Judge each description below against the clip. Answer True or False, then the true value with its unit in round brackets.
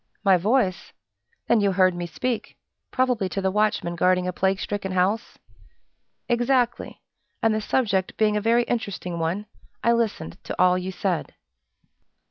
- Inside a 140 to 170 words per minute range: True (150 wpm)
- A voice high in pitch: True (200 Hz)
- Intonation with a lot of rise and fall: False (3.8 semitones)